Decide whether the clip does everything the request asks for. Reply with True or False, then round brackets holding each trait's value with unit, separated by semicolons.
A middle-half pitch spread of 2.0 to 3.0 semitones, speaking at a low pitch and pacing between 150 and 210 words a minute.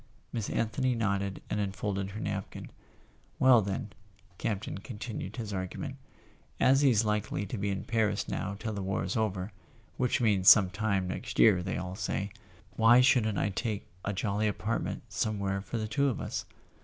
True (2.4 semitones; 105 Hz; 170 wpm)